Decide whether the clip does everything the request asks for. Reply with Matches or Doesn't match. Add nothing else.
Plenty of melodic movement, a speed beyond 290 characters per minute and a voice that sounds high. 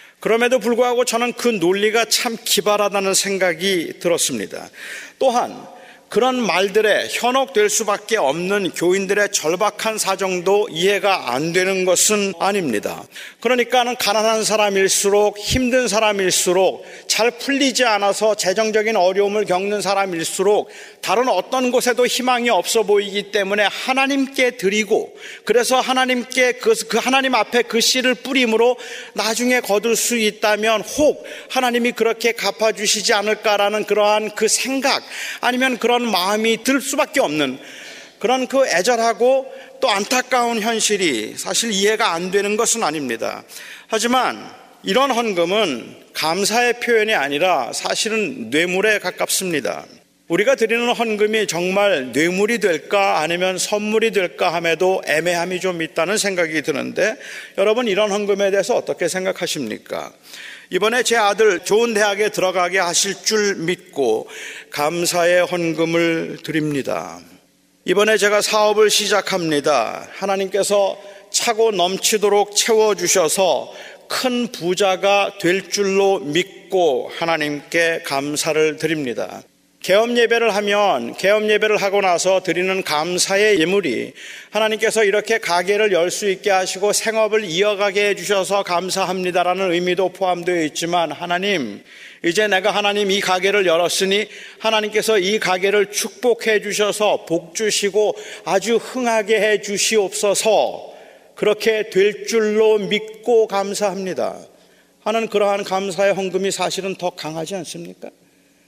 Doesn't match